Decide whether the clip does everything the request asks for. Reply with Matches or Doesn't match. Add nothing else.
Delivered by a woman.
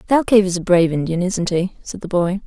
Matches